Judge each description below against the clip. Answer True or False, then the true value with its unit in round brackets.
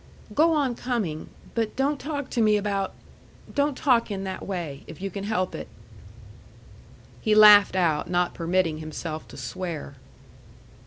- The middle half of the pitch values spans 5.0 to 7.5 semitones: True (5.4 semitones)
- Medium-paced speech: True (150 wpm)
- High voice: True (195 Hz)